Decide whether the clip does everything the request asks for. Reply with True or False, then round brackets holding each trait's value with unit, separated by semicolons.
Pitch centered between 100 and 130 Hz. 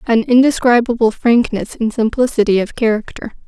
False (230 Hz)